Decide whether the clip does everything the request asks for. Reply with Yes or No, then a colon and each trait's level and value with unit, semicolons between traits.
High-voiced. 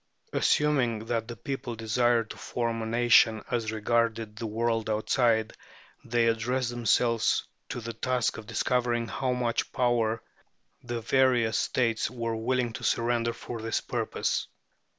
No: low, 115 Hz